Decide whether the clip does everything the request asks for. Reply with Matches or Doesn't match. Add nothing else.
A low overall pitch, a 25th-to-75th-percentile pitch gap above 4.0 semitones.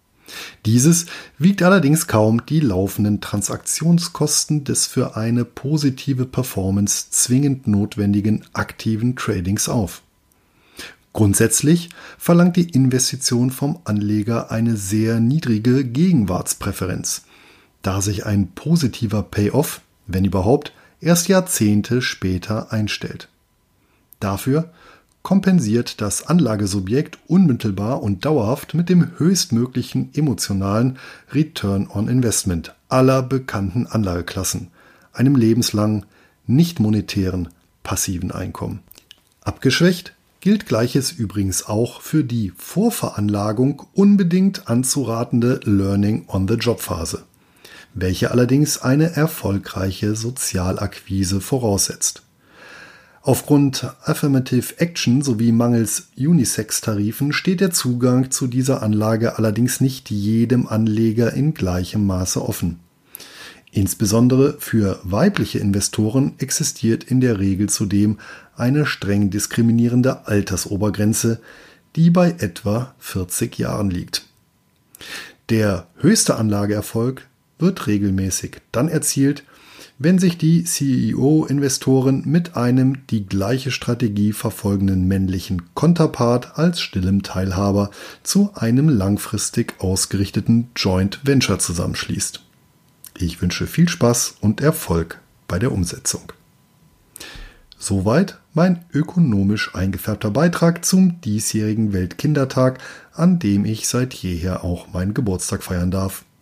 Matches